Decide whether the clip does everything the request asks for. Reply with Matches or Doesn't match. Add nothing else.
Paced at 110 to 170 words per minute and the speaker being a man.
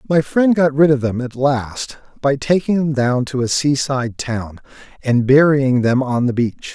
Doesn't match